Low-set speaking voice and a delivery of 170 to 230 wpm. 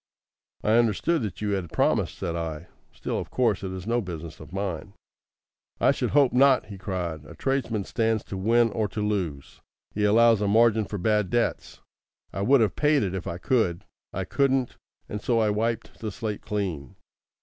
Yes: low, 105 Hz; average, 190 wpm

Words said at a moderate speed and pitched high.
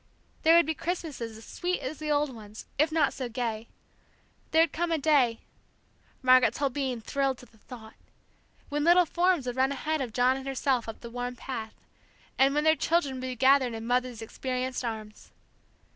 Yes: average, 190 wpm; very high, 260 Hz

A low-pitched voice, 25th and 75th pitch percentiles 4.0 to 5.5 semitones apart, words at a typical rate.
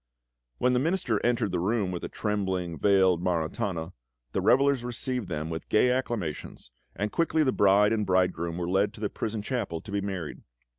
Yes: low, 100 Hz; average, 4.9 semitones; average, 185 wpm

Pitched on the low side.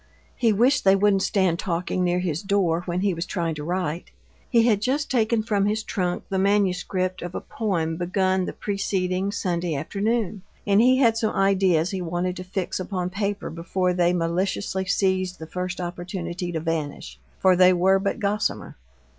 No: medium, 185 Hz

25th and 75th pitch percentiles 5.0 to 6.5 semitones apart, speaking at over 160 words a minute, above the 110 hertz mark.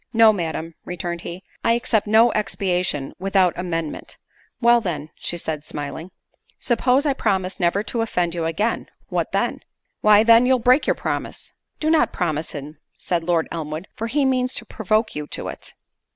Yes: wide, 5.6 semitones; average, 170 wpm; high, 190 Hz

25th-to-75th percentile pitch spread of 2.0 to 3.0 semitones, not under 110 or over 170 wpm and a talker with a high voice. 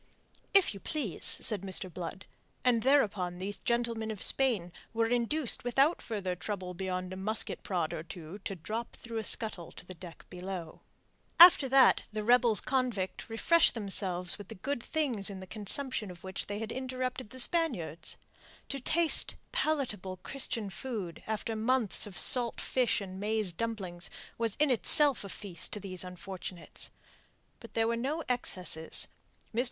No: average, 5.1 semitones; average, 160 wpm; high, 215 Hz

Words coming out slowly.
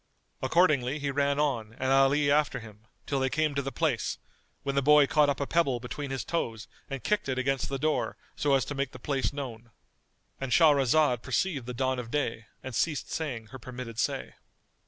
No: average, 200 wpm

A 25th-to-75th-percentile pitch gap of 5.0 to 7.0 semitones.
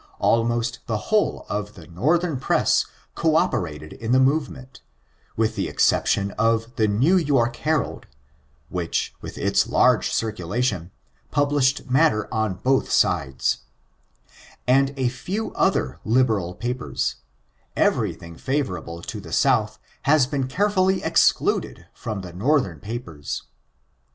Yes: wide, 5.5 semitones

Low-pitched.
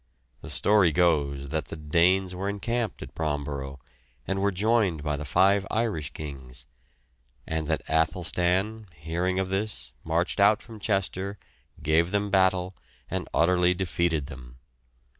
Yes: very low, 90 Hz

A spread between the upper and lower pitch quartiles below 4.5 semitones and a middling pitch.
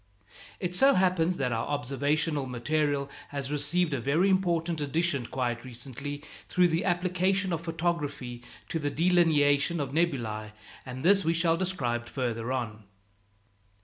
No: average, 4.9 semitones; medium, 150 Hz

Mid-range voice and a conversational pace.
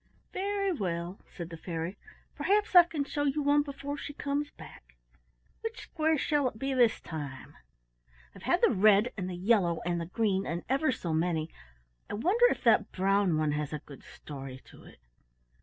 No: high, 205 Hz; average, 185 wpm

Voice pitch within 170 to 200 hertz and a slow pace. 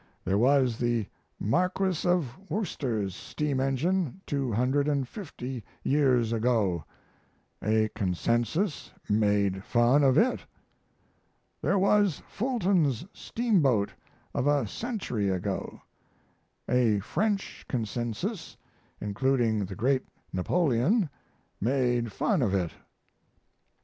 No: low, 130 Hz; slow, 90 wpm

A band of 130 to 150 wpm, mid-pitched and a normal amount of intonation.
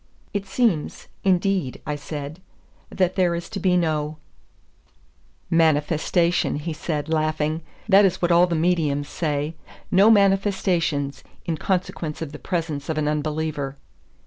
Yes: average, 140 wpm; medium, 160 Hz; average, 3.3 semitones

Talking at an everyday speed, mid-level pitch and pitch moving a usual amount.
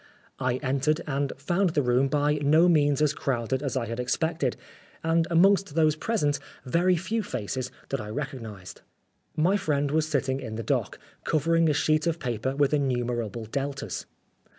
Yes: average, 170 wpm; medium, 145 Hz; average, 3.7 semitones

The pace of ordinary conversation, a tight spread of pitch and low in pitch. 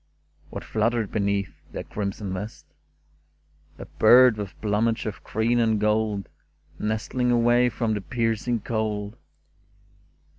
No: slow, 115 wpm; narrow, 2.2 semitones; low, 110 Hz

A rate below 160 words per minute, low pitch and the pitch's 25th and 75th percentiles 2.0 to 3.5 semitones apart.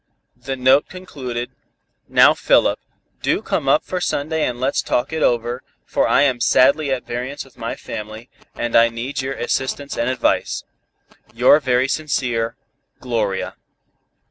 Yes: average, 145 wpm; low, 130 Hz; average, 2.8 semitones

